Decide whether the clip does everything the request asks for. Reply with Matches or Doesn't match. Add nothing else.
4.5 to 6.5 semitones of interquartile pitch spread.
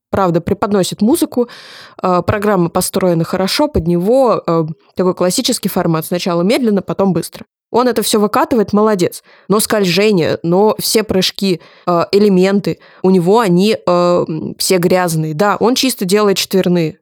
Doesn't match